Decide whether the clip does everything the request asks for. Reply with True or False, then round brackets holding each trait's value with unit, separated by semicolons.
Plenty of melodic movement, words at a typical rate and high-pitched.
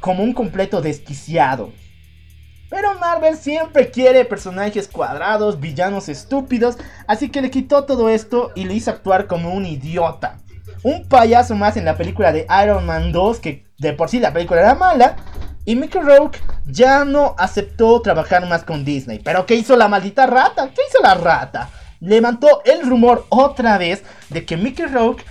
True (7.5 semitones; 170 wpm; 210 Hz)